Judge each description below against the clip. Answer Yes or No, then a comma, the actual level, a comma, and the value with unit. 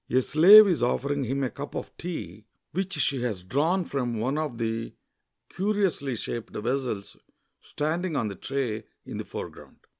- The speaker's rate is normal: Yes, average, 170 wpm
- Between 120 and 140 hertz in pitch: Yes, low, 135 Hz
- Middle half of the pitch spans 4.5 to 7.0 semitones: Yes, wide, 5.5 semitones